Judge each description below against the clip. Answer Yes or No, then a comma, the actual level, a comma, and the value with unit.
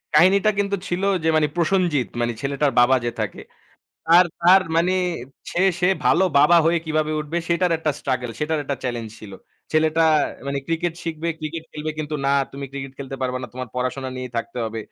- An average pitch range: Yes, average, 4.4 semitones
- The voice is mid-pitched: Yes, medium, 150 Hz